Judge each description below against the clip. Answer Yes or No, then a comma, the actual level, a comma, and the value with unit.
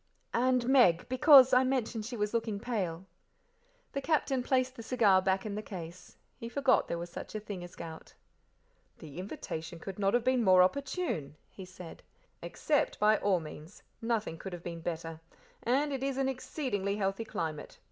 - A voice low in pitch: No, high, 210 Hz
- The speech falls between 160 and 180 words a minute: Yes, average, 175 wpm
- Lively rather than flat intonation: Yes, wide, 6.2 semitones